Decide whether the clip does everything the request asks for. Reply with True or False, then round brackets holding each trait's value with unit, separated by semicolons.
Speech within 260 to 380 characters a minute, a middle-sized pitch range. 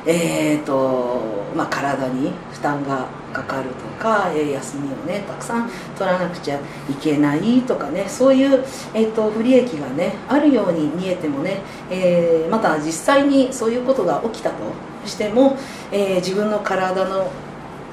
False (295 characters per minute; 7.0 semitones)